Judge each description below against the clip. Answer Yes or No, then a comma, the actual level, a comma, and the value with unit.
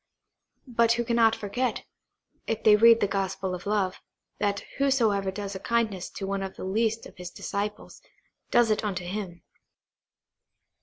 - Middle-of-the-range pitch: No, high, 210 Hz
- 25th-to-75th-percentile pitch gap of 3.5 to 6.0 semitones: No, average, 2.8 semitones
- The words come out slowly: No, average, 155 wpm